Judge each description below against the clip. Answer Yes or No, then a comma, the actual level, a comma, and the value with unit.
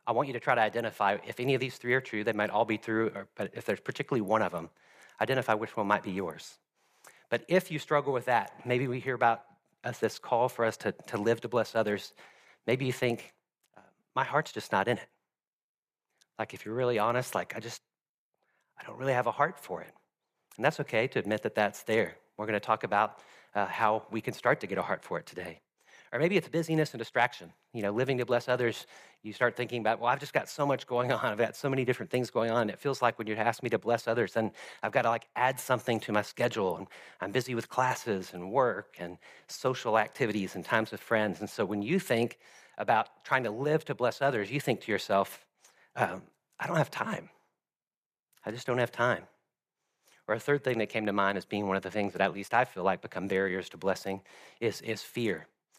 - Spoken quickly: Yes, fast, 240 wpm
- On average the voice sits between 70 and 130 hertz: Yes, low, 115 Hz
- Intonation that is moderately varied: Yes, average, 3.2 semitones